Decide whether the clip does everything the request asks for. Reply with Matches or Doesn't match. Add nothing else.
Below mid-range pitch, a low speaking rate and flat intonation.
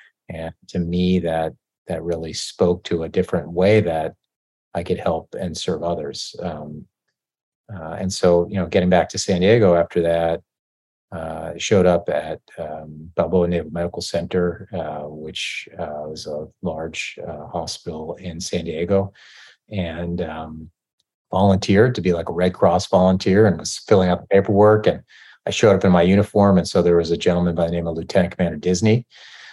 Doesn't match